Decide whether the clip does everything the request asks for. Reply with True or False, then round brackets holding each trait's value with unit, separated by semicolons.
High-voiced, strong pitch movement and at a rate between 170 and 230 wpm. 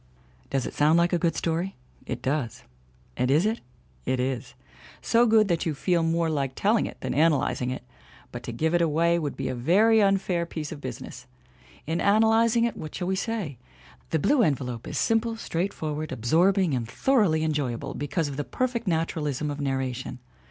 False (160 Hz; 5.9 semitones; 185 wpm)